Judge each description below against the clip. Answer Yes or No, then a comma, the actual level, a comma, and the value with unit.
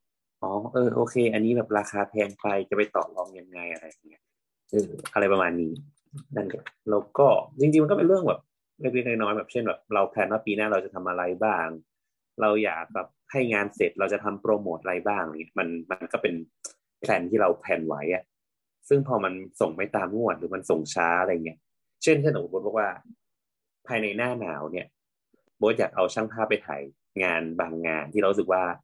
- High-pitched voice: No, low, 105 Hz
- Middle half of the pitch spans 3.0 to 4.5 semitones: No, average, 4.9 semitones